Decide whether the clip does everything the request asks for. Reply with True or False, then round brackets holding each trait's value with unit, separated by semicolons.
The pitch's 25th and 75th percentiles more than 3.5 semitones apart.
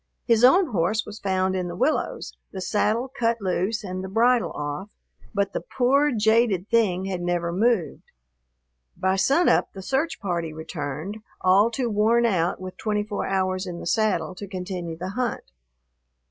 True (4.0 semitones)